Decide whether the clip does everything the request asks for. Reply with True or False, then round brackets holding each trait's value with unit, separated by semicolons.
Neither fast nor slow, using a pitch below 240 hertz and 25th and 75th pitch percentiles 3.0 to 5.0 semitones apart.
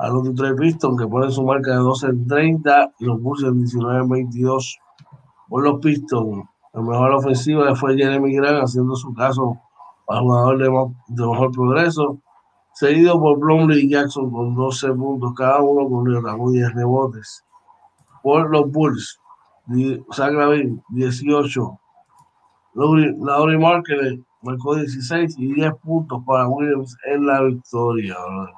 False (145 wpm; 135 Hz; 2.5 semitones)